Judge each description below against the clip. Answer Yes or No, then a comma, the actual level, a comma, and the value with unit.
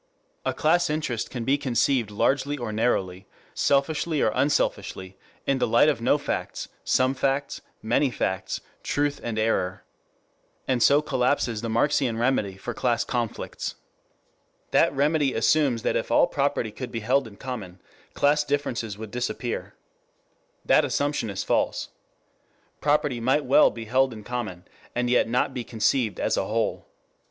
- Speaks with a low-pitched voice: Yes, low, 125 Hz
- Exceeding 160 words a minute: No, average, 150 wpm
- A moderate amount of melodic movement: Yes, average, 4.1 semitones